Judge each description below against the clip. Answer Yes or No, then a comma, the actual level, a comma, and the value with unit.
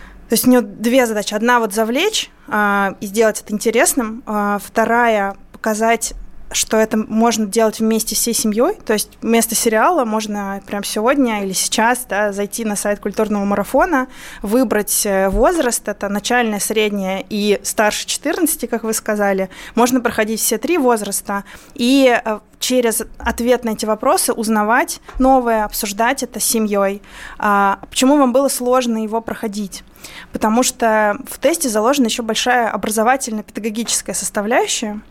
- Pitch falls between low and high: No, high, 225 Hz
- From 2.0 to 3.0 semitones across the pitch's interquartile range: Yes, average, 2.7 semitones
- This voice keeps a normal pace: Yes, average, 145 wpm